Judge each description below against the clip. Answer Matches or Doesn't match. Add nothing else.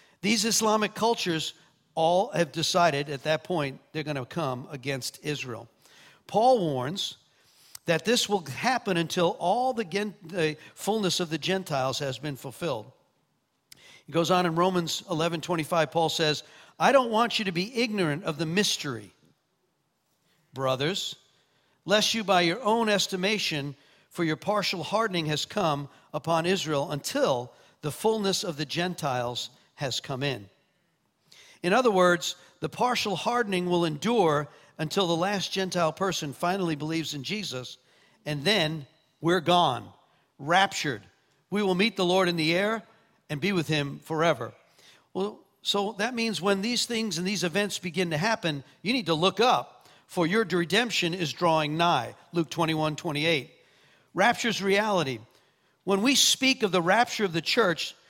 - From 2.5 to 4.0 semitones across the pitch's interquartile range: Doesn't match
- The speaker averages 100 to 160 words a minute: Matches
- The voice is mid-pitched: Matches